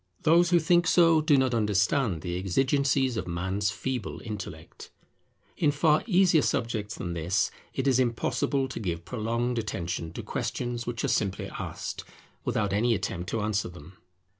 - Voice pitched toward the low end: Yes, low, 115 Hz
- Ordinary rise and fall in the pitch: No, wide, 6.0 semitones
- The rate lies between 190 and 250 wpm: No, average, 160 wpm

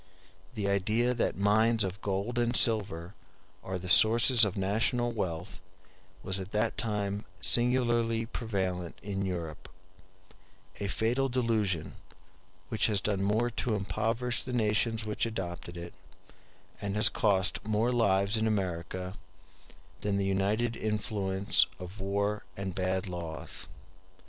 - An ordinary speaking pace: No, slow, 130 wpm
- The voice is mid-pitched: No, low, 105 Hz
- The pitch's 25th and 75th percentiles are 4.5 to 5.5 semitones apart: No, average, 3.1 semitones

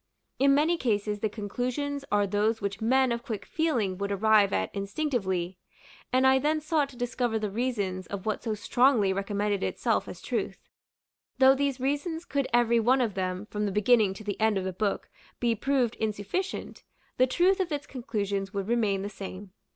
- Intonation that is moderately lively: Yes, average, 4.7 semitones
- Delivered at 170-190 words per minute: Yes, average, 185 wpm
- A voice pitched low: No, high, 220 Hz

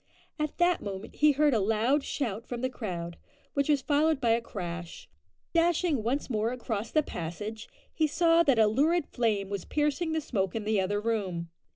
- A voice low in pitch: No, high, 235 Hz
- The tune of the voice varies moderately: No, wide, 6.5 semitones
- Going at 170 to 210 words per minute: Yes, average, 190 wpm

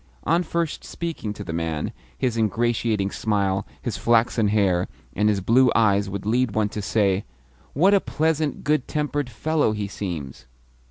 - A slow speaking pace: No, average, 160 wpm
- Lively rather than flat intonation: Yes, wide, 5.9 semitones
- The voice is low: Yes, low, 110 Hz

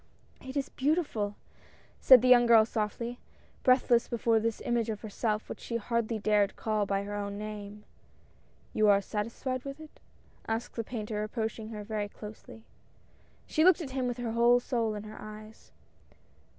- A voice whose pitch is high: Yes, high, 225 Hz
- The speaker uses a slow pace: No, average, 175 wpm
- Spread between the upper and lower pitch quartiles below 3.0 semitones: Yes, narrow, 2.4 semitones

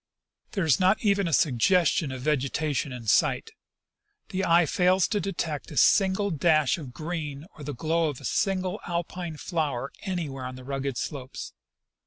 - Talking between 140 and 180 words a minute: Yes, average, 170 wpm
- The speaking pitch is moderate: Yes, medium, 160 Hz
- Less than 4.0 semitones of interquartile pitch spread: No, average, 4.8 semitones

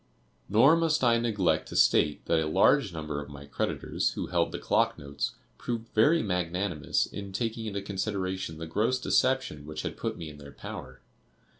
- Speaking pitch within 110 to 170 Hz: No, very low, 95 Hz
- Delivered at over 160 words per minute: Yes, average, 180 wpm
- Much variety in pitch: Yes, wide, 6.8 semitones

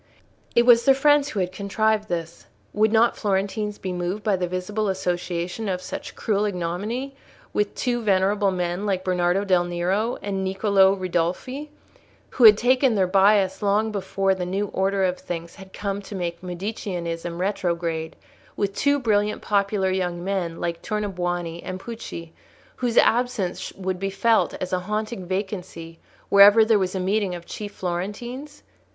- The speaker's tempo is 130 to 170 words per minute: Yes, average, 160 wpm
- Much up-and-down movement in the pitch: No, average, 2.9 semitones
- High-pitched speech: Yes, high, 195 Hz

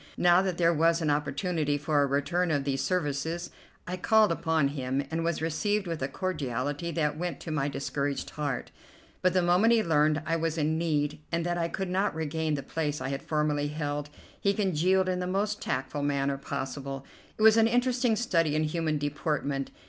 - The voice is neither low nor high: Yes, medium, 160 Hz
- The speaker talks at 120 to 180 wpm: No, average, 195 wpm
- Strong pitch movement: No, average, 3.6 semitones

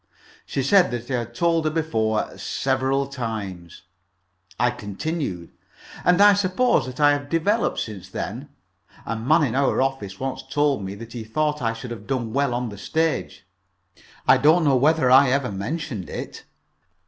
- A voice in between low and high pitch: No, low, 130 Hz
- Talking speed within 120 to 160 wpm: No, average, 170 wpm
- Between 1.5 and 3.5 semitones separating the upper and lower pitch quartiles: No, average, 5.3 semitones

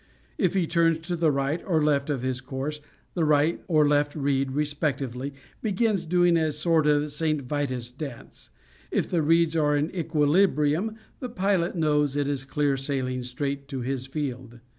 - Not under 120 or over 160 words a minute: No, average, 170 wpm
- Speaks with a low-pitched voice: No, medium, 150 Hz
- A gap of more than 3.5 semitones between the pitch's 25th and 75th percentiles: No, average, 3.2 semitones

